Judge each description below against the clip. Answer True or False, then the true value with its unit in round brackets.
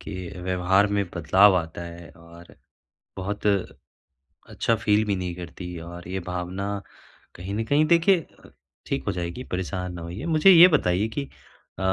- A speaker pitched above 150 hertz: False (95 Hz)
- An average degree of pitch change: True (3.0 semitones)